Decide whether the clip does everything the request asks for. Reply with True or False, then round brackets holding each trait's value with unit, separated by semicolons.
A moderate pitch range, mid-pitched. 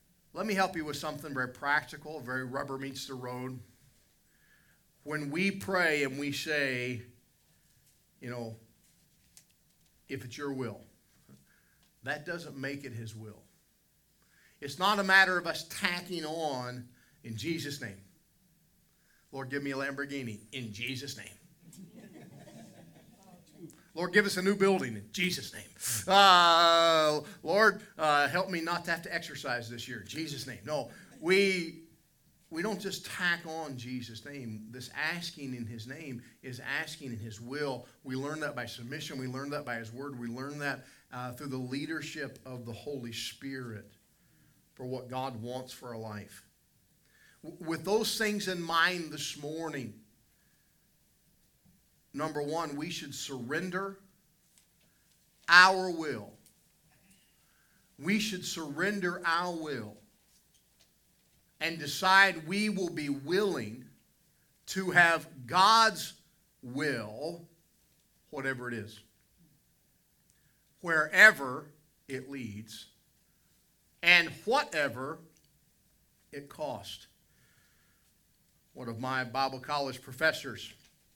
True (4.8 semitones; 145 Hz)